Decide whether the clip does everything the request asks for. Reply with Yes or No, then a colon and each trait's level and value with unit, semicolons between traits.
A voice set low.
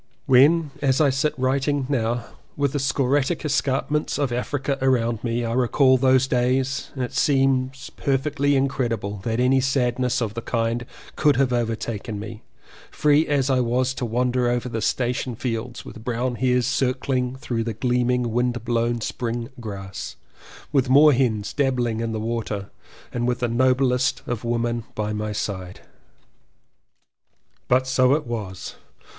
Yes: low, 125 Hz